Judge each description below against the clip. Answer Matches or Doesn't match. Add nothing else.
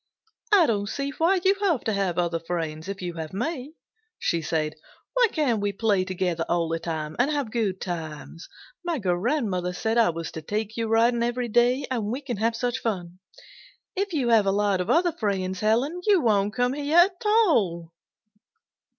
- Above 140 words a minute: Matches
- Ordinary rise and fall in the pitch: Doesn't match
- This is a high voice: Matches